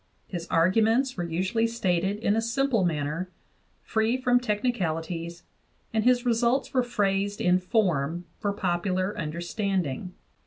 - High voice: Yes, high, 200 Hz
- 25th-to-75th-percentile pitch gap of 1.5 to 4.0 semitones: No, average, 4.8 semitones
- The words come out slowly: Yes, slow, 125 wpm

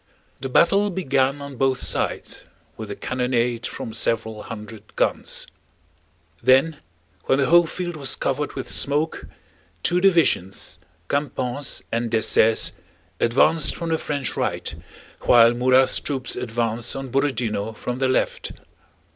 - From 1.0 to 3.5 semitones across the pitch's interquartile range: No, average, 3.9 semitones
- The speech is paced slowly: Yes, slow, 130 wpm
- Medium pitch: No, low, 130 Hz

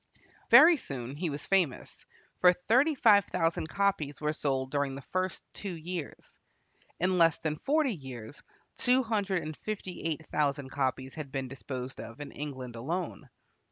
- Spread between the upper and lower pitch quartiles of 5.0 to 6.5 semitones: Yes, wide, 5.6 semitones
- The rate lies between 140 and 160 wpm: Yes, average, 155 wpm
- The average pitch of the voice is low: No, medium, 155 Hz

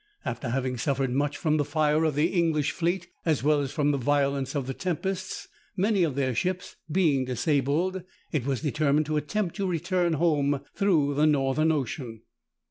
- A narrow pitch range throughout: No, average, 3.6 semitones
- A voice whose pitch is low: No, medium, 150 Hz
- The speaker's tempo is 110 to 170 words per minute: No, average, 180 wpm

